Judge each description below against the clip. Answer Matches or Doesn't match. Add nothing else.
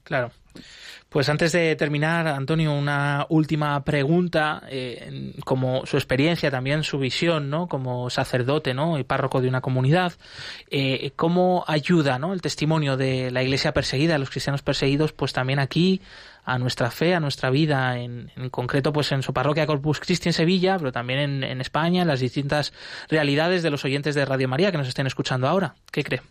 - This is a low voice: Doesn't match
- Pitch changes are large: Doesn't match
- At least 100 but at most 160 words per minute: Doesn't match